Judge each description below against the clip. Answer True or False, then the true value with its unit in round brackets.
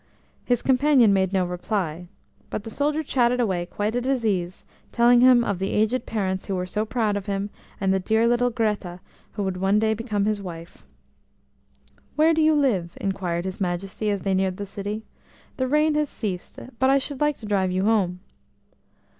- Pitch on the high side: True (210 Hz)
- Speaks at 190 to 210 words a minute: True (195 wpm)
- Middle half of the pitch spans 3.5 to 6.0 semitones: True (4.4 semitones)